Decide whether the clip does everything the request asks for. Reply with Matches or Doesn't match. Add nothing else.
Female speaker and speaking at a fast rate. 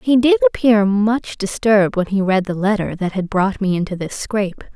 Matches